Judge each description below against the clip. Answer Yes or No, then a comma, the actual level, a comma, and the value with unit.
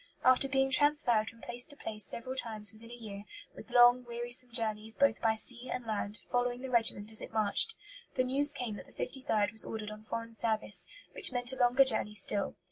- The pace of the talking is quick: Yes, fast, 210 wpm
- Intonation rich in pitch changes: No, average, 2.7 semitones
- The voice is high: Yes, high, 235 Hz